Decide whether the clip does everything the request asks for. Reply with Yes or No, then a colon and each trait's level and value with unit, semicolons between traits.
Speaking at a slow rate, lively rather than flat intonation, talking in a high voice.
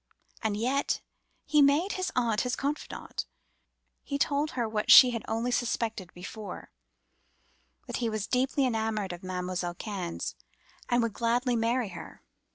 No: slow, 130 wpm; average, 3.4 semitones; high, 230 Hz